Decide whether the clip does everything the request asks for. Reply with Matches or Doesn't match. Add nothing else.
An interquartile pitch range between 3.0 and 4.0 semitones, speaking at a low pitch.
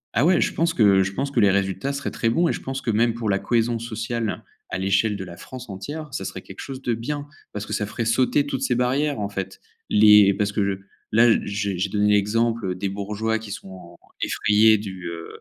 Matches